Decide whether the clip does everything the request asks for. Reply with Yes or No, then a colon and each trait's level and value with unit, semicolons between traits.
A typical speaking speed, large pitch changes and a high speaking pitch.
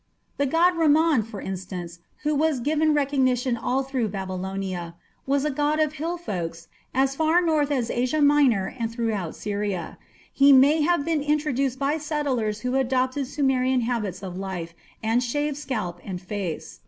Yes: average, 160 wpm; wide, 6.4 semitones; very high, 260 Hz